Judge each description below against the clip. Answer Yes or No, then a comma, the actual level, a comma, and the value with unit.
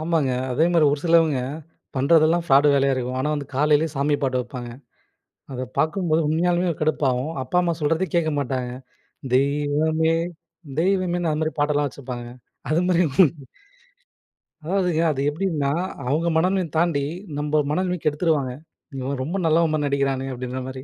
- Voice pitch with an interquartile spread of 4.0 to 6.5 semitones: No, average, 3.4 semitones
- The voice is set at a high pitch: No, medium, 150 Hz